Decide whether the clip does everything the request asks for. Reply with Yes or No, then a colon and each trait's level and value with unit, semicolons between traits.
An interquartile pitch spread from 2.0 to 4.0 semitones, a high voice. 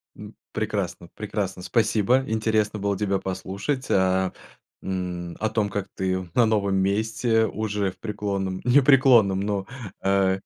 No: narrow, 2.6 semitones; low, 100 Hz